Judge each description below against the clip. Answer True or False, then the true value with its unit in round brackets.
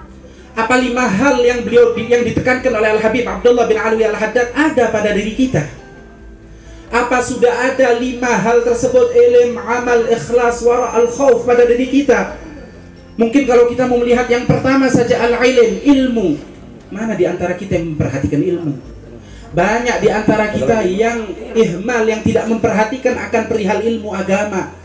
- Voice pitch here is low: False (235 Hz)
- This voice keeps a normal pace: False (155 wpm)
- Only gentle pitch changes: True (2.2 semitones)